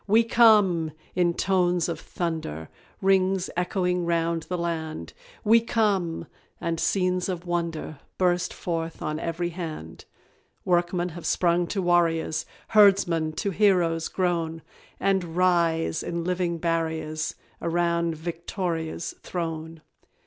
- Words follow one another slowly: Yes, slow, 115 wpm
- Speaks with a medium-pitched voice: Yes, medium, 170 Hz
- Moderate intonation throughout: No, narrow, 1.8 semitones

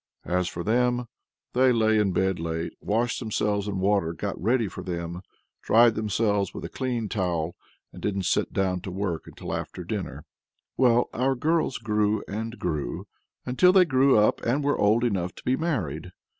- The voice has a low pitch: Yes, low, 105 Hz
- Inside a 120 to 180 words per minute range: Yes, average, 175 wpm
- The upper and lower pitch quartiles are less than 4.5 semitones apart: No, average, 5.0 semitones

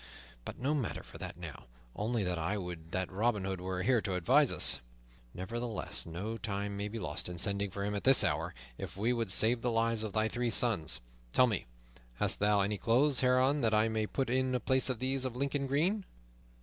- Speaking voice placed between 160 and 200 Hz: No, low, 110 Hz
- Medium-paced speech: No, fast, 215 wpm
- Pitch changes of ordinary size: Yes, average, 4.5 semitones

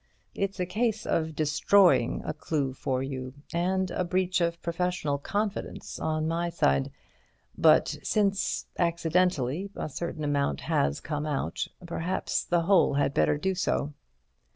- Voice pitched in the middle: Yes, medium, 170 Hz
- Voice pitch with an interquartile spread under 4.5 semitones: Yes, average, 4.0 semitones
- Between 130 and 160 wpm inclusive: Yes, slow, 135 wpm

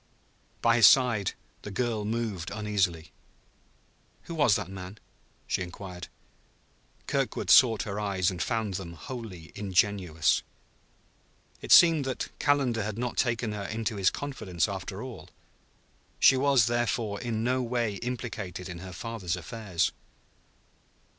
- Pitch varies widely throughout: No, average, 4.1 semitones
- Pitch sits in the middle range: No, low, 105 Hz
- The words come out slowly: Yes, slow, 130 wpm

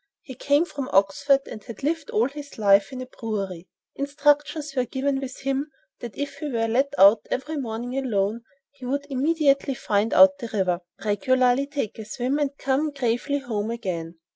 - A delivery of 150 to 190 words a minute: Yes, average, 180 wpm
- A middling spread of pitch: Yes, average, 4.3 semitones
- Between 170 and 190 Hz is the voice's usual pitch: No, very high, 260 Hz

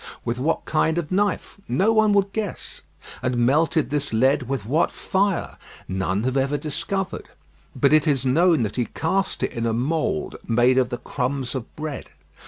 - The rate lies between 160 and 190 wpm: Yes, average, 180 wpm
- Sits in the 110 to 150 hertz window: Yes, medium, 140 Hz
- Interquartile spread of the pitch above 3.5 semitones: Yes, average, 5.3 semitones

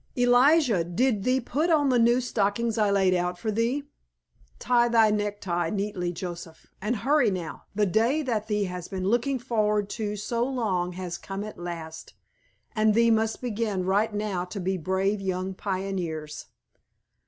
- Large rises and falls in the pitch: No, average, 4.1 semitones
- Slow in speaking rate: No, average, 165 wpm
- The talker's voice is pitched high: Yes, high, 210 Hz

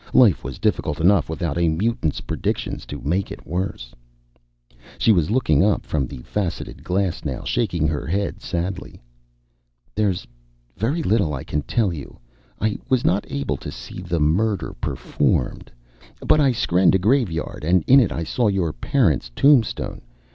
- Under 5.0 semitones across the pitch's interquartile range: No, wide, 5.6 semitones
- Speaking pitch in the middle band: No, very low, 90 Hz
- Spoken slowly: No, average, 160 wpm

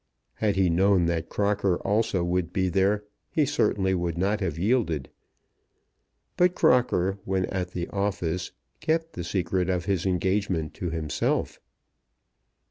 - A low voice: Yes, very low, 95 Hz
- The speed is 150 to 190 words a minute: No, slow, 135 wpm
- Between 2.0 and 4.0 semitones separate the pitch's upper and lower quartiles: Yes, average, 2.8 semitones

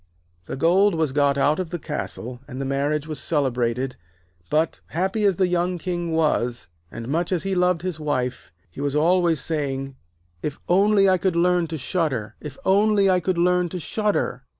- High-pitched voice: No, medium, 160 Hz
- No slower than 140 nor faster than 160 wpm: No, average, 190 wpm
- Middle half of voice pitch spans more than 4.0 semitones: Yes, average, 4.7 semitones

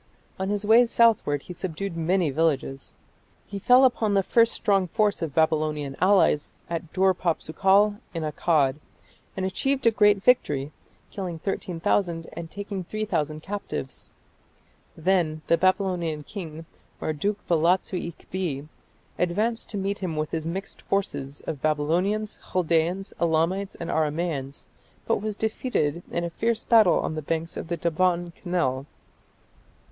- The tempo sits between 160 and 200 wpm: No, average, 140 wpm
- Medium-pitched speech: Yes, medium, 175 Hz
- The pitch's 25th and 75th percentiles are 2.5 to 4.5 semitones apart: Yes, average, 4.1 semitones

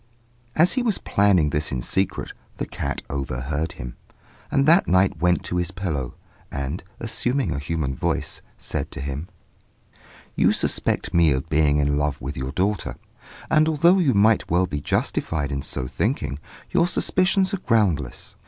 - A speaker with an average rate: Yes, average, 160 wpm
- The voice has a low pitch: Yes, very low, 85 Hz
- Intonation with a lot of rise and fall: Yes, wide, 8.4 semitones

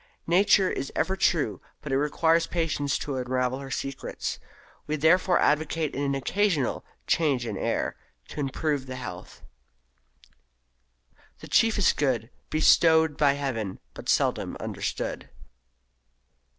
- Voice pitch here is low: No, medium, 145 Hz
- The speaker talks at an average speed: No, slow, 120 wpm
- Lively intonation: No, average, 3.6 semitones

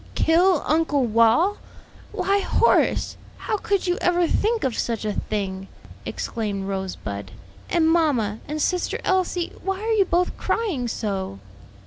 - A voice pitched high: Yes, very high, 315 Hz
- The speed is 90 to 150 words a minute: Yes, slow, 135 wpm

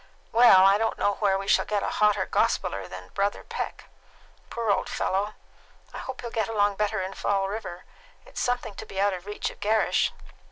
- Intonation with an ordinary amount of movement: No, narrow, 2.1 semitones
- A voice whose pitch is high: Yes, high, 205 Hz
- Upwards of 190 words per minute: Yes, fast, 205 wpm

